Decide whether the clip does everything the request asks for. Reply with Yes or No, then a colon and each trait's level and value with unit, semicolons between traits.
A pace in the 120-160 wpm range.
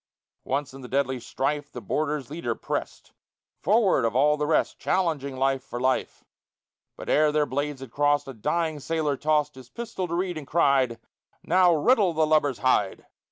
No: average, 175 wpm